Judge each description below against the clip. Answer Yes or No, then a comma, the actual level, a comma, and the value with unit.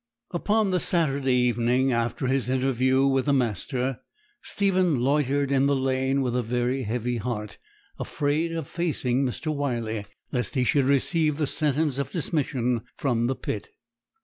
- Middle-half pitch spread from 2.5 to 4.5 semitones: Yes, average, 2.8 semitones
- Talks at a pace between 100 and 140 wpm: No, average, 150 wpm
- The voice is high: No, low, 135 Hz